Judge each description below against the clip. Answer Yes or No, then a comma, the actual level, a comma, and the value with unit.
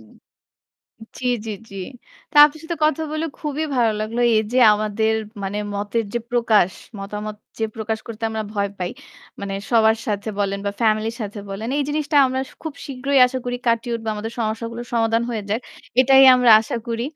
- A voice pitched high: Yes, high, 225 Hz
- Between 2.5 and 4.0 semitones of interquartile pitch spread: Yes, average, 2.8 semitones